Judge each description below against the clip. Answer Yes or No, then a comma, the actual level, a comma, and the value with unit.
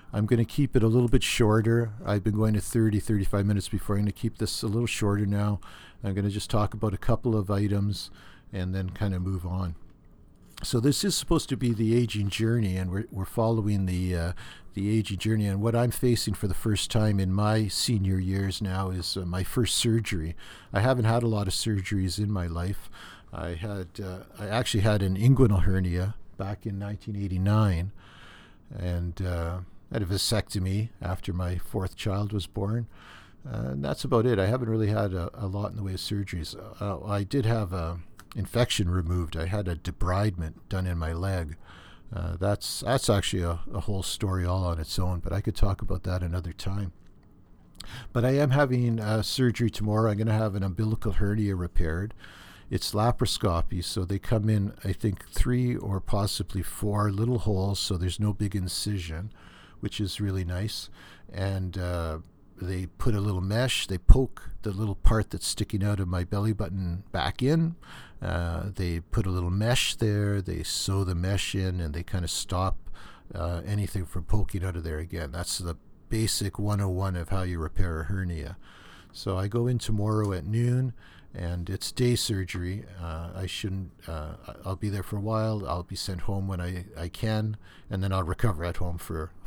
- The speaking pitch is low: Yes, low, 100 Hz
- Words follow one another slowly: No, average, 195 wpm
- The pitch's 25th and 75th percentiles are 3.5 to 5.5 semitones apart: No, average, 3.0 semitones